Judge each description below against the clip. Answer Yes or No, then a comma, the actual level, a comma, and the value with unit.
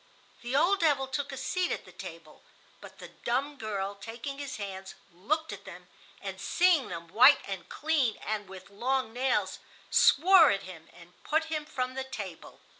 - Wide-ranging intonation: Yes, wide, 6.8 semitones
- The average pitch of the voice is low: No, very high, 255 Hz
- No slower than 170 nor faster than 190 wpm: Yes, average, 180 wpm